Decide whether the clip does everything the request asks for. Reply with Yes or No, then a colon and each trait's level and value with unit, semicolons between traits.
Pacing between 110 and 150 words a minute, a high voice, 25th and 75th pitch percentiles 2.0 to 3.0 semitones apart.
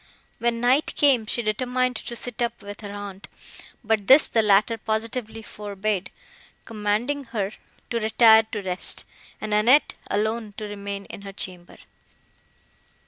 Yes: average, 140 wpm; high, 215 Hz; narrow, 2.6 semitones